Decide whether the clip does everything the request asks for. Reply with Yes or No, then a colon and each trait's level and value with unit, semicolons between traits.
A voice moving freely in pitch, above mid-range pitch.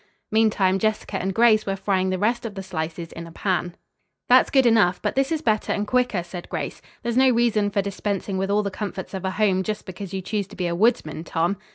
No: average, 2.7 semitones; high, 200 Hz